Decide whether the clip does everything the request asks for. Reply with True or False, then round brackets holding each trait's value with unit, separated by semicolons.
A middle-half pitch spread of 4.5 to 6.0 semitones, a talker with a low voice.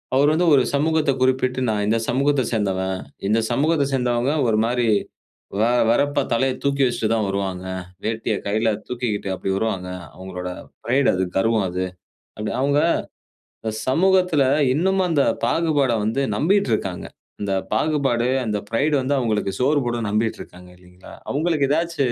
True (5.1 semitones; 120 Hz)